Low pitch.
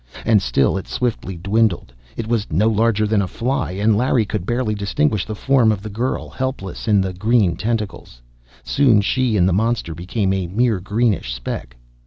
Yes: low, 105 Hz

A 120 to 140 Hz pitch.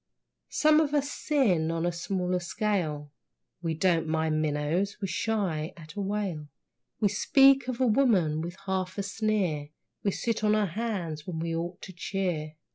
No: medium, 185 Hz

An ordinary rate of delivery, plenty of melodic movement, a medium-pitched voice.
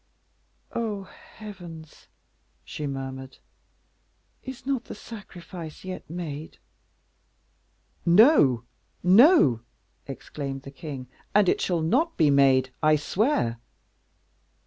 No: slow, 95 wpm; wide, 7.2 semitones; medium, 160 Hz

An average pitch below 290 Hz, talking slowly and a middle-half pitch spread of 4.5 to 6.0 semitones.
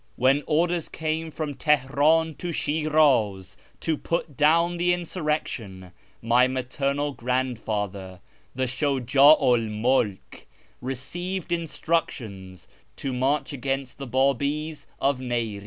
No: low, 135 Hz; slow, 105 wpm; average, 4.1 semitones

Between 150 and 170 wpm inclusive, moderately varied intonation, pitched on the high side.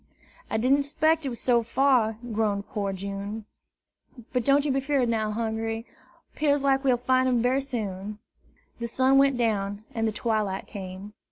Yes: average, 165 wpm; average, 4.1 semitones; high, 230 Hz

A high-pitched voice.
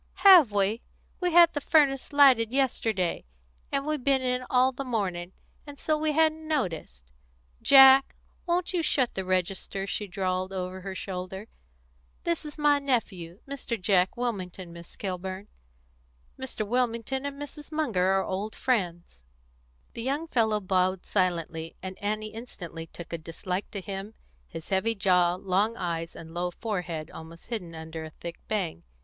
Yes: high, 205 Hz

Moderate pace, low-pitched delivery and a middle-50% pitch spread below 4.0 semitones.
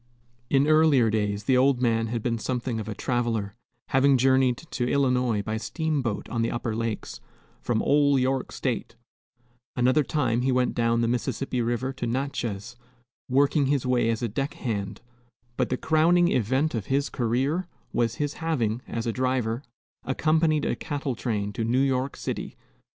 Yes: average, 165 wpm; low, 125 Hz; average, 3.1 semitones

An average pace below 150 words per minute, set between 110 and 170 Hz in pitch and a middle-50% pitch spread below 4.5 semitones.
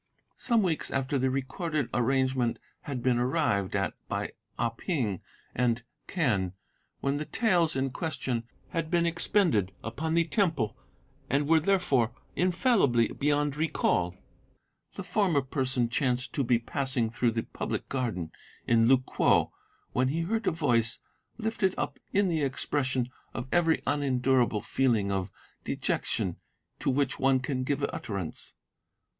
No: average, 140 wpm; low, 135 Hz; average, 5.2 semitones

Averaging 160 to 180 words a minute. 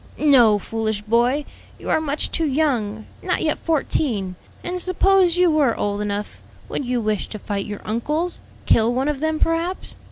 Yes: average, 170 wpm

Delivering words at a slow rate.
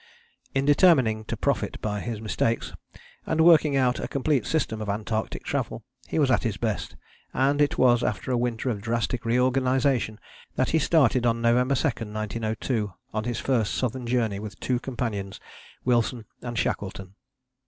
No: average, 165 wpm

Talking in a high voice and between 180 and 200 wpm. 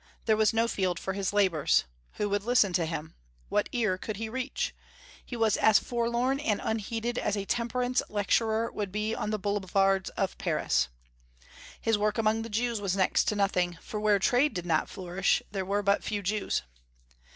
Yes: high, 210 Hz; average, 185 wpm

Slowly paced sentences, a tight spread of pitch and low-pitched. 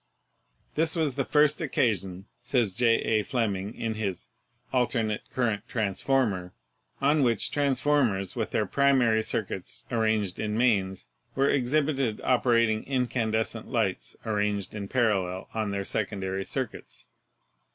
No: slow, 125 wpm; average, 4.3 semitones; low, 110 Hz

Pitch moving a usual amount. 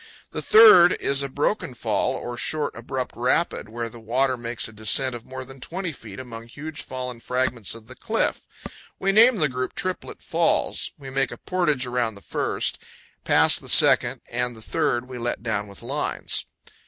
Yes: average, 3.6 semitones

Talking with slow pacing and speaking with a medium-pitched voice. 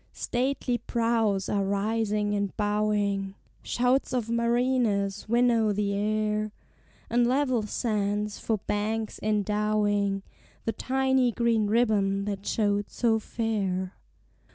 No: slow, 105 wpm; high, 215 Hz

